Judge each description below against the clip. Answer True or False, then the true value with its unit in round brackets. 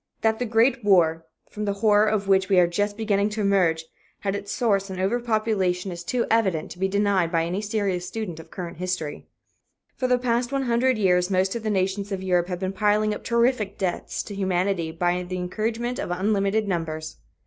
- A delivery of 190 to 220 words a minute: True (205 wpm)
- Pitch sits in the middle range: False (195 Hz)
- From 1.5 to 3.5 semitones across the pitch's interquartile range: True (3.2 semitones)